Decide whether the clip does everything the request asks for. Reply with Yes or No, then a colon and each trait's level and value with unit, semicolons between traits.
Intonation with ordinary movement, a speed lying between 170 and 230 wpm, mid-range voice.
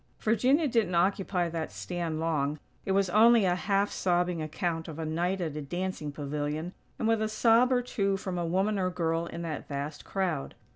Yes: average, 3.7 semitones; average, 195 wpm; medium, 180 Hz